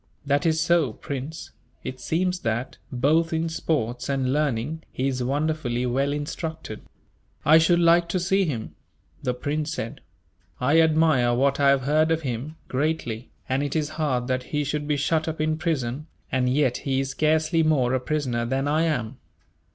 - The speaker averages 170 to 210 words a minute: Yes, average, 175 wpm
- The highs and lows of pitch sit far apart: No, average, 3.7 semitones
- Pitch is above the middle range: No, medium, 145 Hz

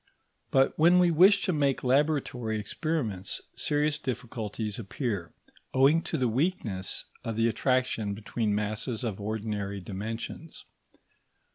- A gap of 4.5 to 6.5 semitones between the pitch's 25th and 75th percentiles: Yes, wide, 5.6 semitones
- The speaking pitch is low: Yes, low, 115 Hz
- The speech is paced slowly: Yes, slow, 120 wpm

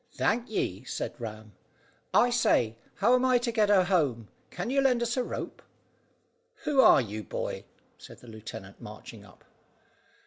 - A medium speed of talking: Yes, average, 165 wpm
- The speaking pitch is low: No, medium, 185 Hz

